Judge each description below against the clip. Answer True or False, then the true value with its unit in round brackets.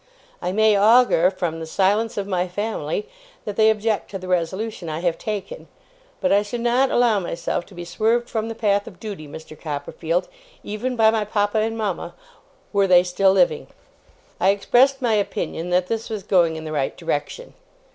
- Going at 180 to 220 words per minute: True (185 wpm)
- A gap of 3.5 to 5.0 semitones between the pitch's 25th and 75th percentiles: True (3.9 semitones)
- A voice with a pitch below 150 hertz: False (200 Hz)